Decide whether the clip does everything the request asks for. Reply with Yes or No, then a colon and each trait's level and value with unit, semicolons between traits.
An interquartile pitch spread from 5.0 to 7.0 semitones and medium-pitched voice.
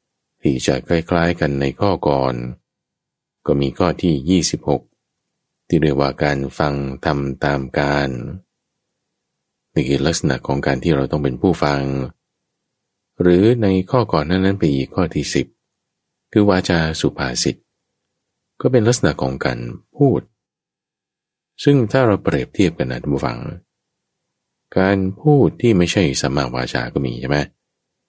No: average, 5.3 semitones; very low, 75 Hz